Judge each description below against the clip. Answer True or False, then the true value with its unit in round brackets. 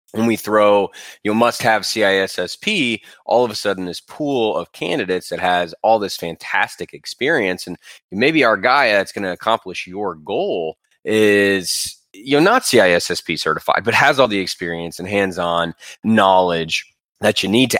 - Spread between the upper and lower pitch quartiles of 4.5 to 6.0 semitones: False (3.5 semitones)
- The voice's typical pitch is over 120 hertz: False (100 Hz)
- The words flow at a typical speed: True (170 wpm)